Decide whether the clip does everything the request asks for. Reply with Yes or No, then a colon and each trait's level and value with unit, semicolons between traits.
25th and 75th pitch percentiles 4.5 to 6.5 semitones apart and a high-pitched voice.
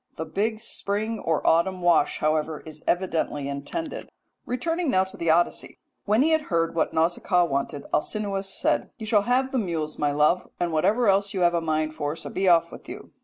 No: average, 5.1 semitones; medium, 175 Hz